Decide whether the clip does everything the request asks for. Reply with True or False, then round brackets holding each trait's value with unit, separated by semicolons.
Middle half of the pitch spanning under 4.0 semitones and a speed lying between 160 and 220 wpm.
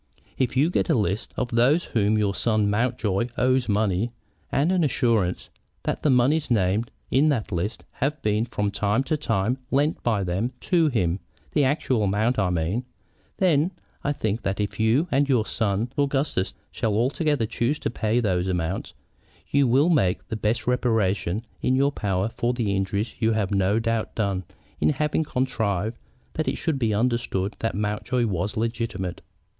False (4.5 semitones; 175 wpm)